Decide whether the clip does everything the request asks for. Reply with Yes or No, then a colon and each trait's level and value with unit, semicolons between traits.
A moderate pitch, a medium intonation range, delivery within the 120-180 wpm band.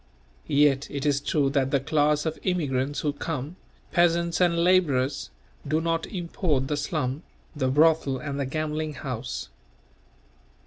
Yes: medium, 150 Hz; average, 3.0 semitones; average, 140 wpm